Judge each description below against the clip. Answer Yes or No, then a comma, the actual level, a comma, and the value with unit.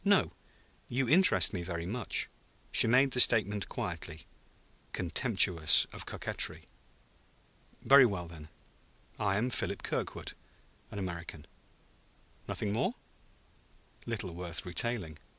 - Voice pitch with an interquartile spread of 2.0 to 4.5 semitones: No, wide, 5.6 semitones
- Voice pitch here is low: Yes, low, 100 Hz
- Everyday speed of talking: No, slow, 110 wpm